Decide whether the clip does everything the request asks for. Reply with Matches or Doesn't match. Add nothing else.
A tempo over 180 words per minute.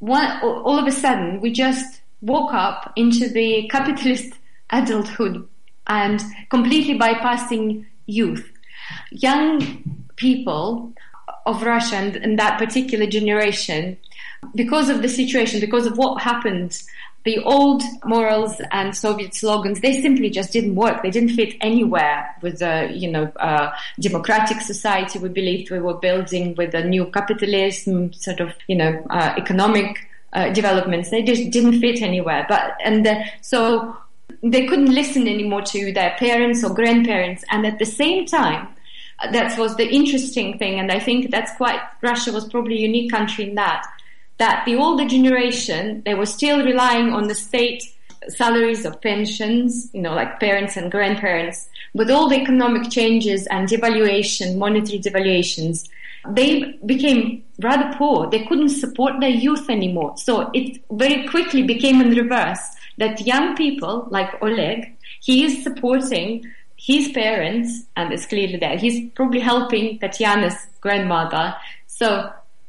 Doesn't match